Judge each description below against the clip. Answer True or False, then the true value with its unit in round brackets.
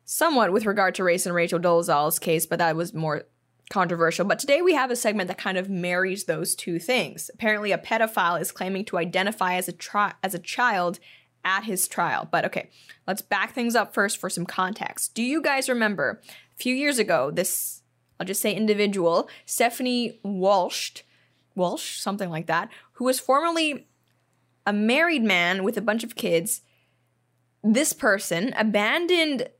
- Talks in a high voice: True (195 Hz)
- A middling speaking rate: True (175 wpm)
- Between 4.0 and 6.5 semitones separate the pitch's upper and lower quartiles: True (4.6 semitones)